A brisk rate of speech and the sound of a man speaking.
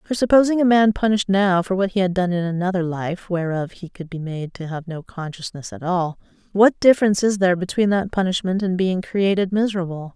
No: fast, 215 wpm; female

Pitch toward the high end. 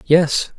No: medium, 155 Hz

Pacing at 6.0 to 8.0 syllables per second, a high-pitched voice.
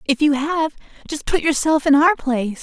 No: 5.1 syllables/s; very high, 290 Hz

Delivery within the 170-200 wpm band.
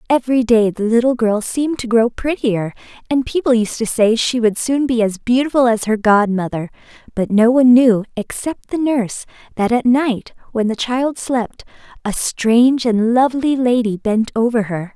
Yes: average, 180 wpm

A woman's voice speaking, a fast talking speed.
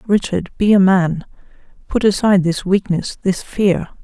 No: female; average, 150 wpm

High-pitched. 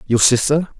No: low, 135 Hz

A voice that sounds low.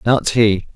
Yes: low, 110 Hz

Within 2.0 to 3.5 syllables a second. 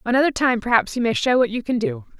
No: 6.5 syllables/s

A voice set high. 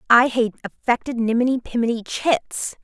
Yes: high, 240 Hz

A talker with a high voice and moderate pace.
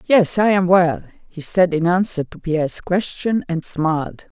No: medium, 175 Hz; average, 180 wpm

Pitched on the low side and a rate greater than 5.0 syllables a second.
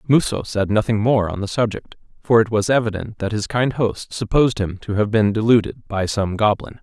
Yes: low, 110 Hz; 5.4 syllables/s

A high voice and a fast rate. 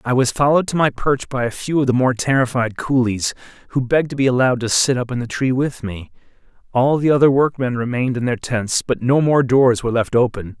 No: low, 125 Hz; fast, 240 wpm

